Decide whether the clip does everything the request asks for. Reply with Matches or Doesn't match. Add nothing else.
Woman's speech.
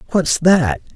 Doesn't match